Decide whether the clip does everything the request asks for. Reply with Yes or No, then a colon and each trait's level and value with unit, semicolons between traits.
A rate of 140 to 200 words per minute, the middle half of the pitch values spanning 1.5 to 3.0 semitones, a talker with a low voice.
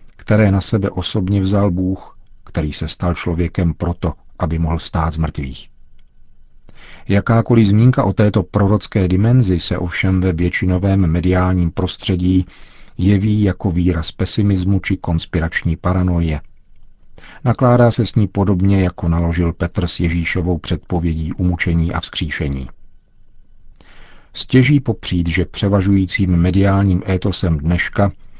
No: average, 120 wpm; narrow, 2.6 semitones; very low, 90 Hz